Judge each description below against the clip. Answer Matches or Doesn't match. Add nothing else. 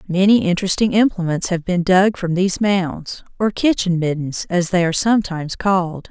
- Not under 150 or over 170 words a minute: Matches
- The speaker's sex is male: Doesn't match